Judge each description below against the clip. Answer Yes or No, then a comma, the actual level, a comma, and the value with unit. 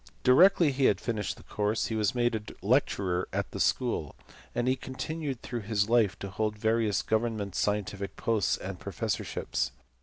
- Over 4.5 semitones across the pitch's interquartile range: No, average, 2.9 semitones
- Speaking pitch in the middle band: No, low, 110 Hz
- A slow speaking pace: No, average, 170 wpm